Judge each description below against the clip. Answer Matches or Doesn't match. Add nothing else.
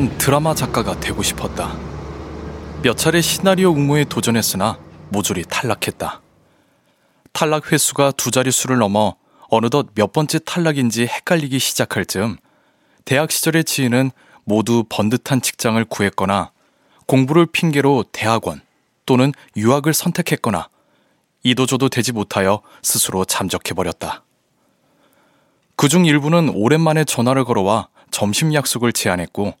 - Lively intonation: Matches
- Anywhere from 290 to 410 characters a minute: Matches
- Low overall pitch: Matches